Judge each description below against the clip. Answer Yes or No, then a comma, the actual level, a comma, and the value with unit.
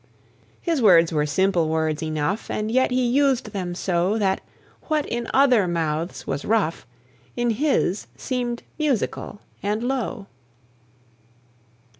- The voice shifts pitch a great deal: Yes, wide, 6.6 semitones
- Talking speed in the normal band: No, slow, 125 wpm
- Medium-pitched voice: No, high, 210 Hz